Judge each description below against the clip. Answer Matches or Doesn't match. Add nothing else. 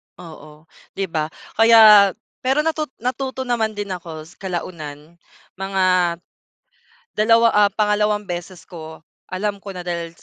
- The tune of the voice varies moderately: Matches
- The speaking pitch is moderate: Doesn't match